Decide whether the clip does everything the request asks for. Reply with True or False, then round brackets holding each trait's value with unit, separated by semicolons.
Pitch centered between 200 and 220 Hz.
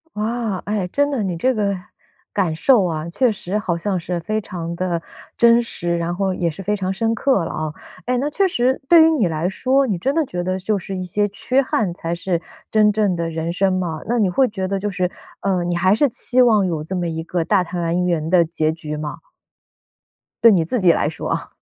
False (185 Hz)